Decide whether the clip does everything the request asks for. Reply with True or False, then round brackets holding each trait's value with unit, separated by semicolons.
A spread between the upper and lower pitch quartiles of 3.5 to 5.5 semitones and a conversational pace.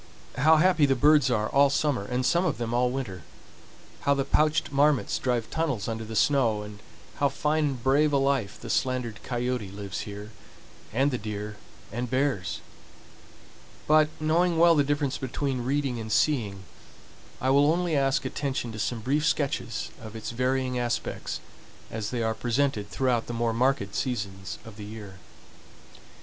True (4.3 semitones; 165 wpm)